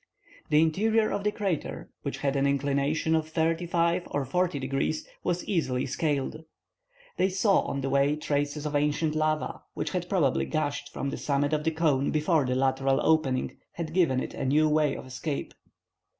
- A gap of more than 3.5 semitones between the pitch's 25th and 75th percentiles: No, average, 3.1 semitones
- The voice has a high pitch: No, medium, 150 Hz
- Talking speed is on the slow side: No, average, 180 wpm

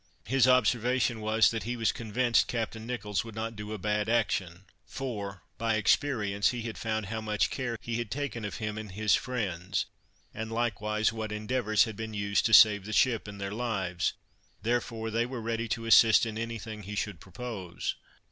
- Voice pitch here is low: Yes, low, 110 Hz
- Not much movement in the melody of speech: Yes, narrow, 1.9 semitones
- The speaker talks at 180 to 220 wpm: Yes, average, 190 wpm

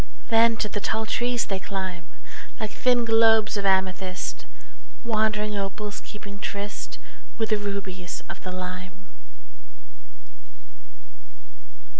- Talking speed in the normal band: No, slow, 110 wpm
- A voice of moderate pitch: No, high, 205 Hz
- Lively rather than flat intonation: No, narrow, 2.6 semitones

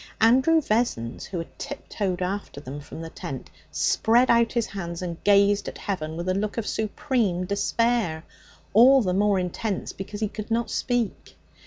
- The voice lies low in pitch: No, high, 200 Hz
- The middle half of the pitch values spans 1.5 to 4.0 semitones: No, average, 4.4 semitones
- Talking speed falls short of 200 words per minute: Yes, average, 170 wpm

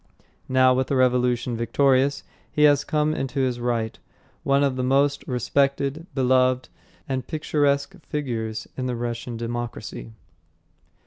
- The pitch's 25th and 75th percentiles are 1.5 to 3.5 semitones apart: Yes, narrow, 2.6 semitones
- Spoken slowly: Yes, slow, 130 wpm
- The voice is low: Yes, low, 130 Hz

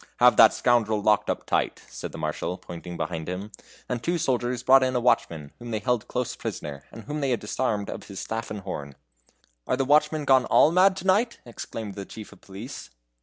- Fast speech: Yes, fast, 215 wpm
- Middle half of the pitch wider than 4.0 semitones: Yes, average, 4.6 semitones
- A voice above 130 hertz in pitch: No, low, 120 Hz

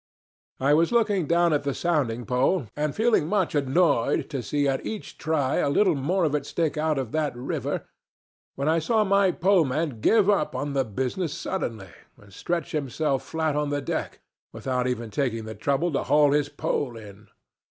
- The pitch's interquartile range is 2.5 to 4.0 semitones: No, average, 4.4 semitones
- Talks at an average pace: Yes, average, 180 wpm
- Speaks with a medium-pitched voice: Yes, medium, 145 Hz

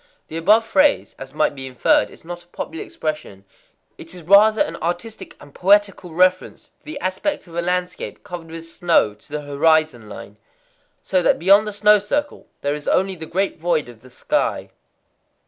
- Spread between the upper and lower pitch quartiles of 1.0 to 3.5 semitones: No, average, 4.3 semitones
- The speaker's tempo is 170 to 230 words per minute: Yes, average, 180 wpm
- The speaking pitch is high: No, medium, 170 Hz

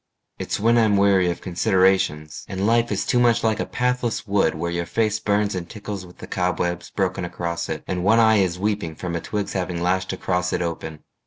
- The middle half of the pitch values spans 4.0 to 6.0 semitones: No, average, 3.4 semitones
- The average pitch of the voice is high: No, very low, 95 Hz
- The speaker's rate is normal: No, fast, 215 wpm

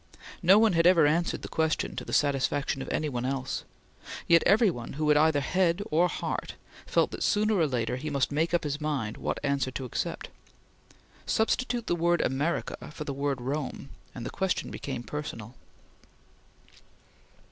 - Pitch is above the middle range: No, medium, 150 Hz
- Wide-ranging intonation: No, average, 4.0 semitones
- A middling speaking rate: Yes, average, 175 wpm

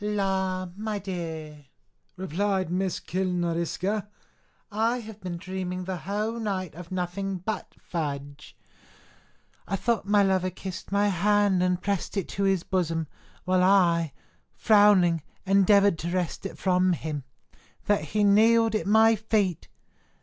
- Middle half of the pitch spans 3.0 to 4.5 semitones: No, narrow, 2.6 semitones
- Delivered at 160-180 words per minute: No, slow, 135 wpm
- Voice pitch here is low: No, high, 190 Hz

